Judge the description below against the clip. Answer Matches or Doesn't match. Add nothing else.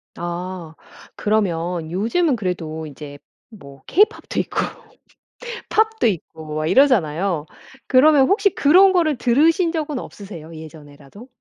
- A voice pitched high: Matches